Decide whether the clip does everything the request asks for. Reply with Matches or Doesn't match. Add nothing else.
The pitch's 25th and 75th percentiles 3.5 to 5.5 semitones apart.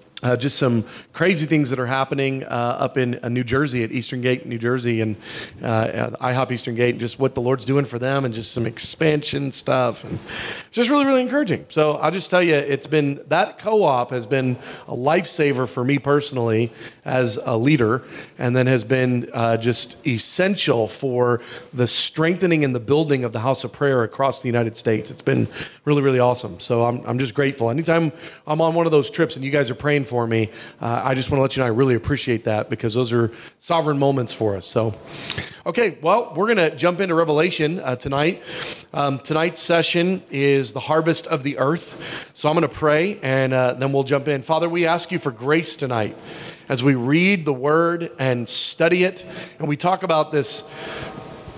Matches